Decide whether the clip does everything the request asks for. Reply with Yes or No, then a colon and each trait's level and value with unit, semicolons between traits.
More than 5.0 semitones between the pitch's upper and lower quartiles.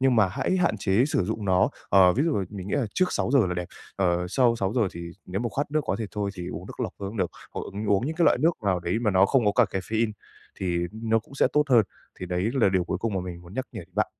No: average, 4.5 semitones